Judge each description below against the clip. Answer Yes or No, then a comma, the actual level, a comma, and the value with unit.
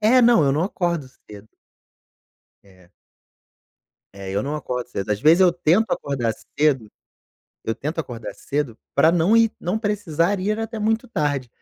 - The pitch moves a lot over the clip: Yes, wide, 8.6 semitones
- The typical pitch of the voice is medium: Yes, medium, 155 Hz